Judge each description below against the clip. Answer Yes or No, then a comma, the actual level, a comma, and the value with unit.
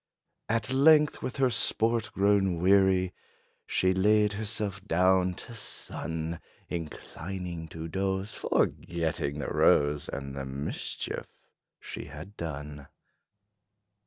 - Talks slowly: Yes, slow, 105 wpm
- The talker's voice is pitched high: No, very low, 95 Hz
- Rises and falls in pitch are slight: No, average, 4.4 semitones